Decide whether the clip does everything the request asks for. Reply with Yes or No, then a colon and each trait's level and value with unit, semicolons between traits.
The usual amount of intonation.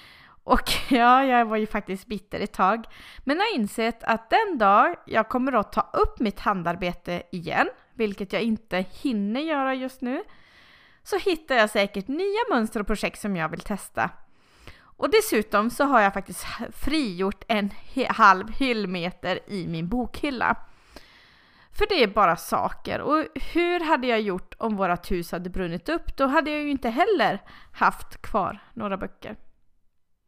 No: wide, 6.1 semitones